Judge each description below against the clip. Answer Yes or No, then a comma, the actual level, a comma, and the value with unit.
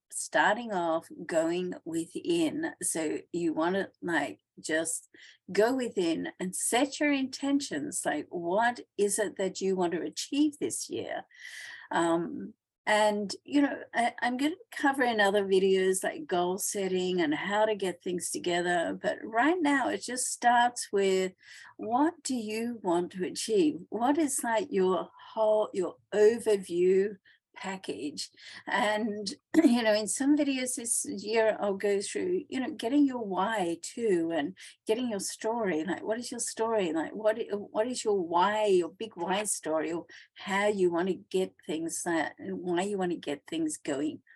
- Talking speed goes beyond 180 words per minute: No, average, 160 wpm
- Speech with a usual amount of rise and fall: No, wide, 7.1 semitones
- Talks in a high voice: Yes, high, 215 Hz